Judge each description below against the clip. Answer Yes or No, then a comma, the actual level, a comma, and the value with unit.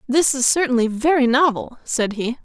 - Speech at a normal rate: Yes, average, 170 wpm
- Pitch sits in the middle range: No, very high, 260 Hz